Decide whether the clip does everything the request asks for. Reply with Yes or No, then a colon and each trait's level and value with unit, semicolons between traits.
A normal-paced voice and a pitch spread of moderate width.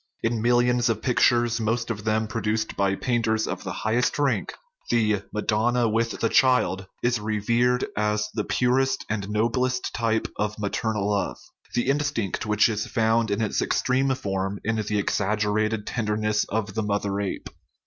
No: average, 165 wpm; narrow, 2.2 semitones